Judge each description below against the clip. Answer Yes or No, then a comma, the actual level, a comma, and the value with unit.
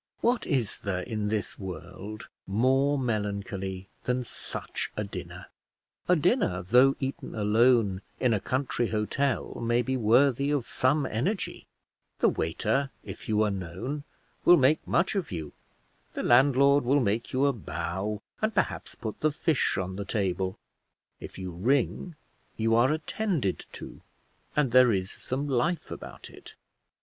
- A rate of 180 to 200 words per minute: No, average, 150 wpm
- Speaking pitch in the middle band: No, low, 120 Hz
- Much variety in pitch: Yes, wide, 5.7 semitones